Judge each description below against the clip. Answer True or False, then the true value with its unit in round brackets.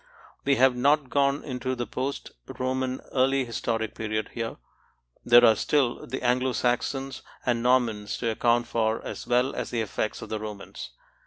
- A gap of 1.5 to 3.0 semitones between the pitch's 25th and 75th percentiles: True (2.4 semitones)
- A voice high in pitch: False (125 Hz)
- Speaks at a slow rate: False (165 wpm)